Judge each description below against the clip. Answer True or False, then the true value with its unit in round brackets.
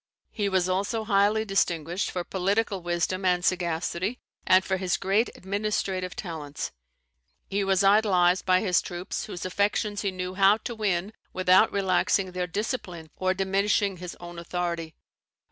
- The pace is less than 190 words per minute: True (145 wpm)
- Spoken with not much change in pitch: True (2.2 semitones)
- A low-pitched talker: False (185 Hz)